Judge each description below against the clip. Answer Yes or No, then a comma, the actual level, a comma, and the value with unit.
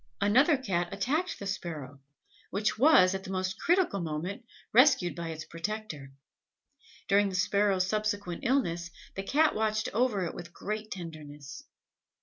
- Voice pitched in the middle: No, high, 195 Hz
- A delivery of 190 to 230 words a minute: No, average, 140 wpm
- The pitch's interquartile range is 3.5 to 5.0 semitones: Yes, average, 4.0 semitones